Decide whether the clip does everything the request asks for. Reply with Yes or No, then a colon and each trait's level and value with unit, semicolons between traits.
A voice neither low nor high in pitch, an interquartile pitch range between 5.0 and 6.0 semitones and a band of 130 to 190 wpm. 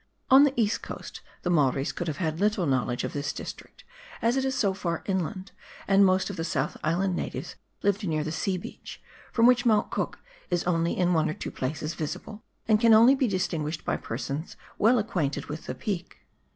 No: medium, 180 Hz; average, 5.3 semitones; fast, 205 wpm